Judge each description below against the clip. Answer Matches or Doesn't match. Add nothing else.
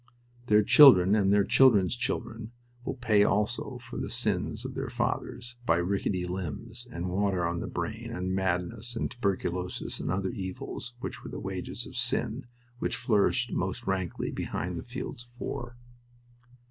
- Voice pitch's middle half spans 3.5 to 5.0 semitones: Matches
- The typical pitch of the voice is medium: Doesn't match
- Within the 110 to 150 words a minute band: Doesn't match